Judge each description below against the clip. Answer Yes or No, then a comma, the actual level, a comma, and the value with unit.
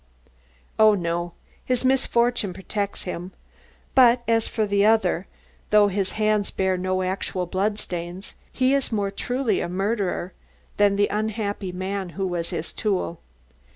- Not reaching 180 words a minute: Yes, average, 140 wpm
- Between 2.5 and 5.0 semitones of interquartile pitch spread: Yes, average, 2.9 semitones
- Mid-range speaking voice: No, high, 200 Hz